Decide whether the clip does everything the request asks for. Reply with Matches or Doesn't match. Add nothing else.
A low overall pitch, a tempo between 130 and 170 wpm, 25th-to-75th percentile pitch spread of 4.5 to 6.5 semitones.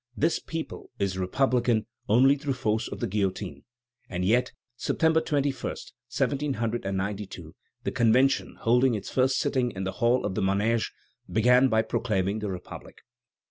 Matches